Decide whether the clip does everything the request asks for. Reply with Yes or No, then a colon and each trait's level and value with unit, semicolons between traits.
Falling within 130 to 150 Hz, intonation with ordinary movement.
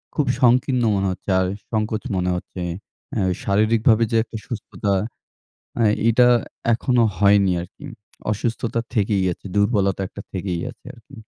No: low, 105 Hz; average, 3.1 semitones